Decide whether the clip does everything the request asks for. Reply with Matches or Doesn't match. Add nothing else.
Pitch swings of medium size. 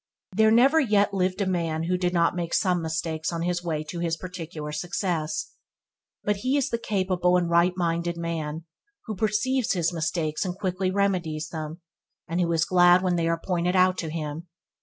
Doesn't match